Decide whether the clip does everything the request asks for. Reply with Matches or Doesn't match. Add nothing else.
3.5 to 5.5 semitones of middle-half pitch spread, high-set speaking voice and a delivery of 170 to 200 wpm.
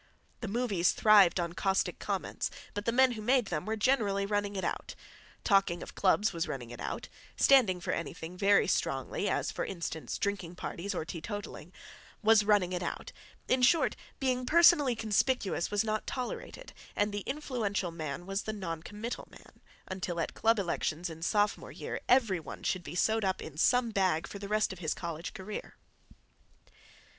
Matches